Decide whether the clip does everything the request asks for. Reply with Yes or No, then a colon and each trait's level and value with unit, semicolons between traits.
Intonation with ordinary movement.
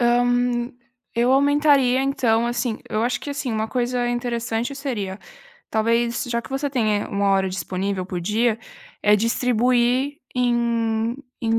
No: narrow, 2.1 semitones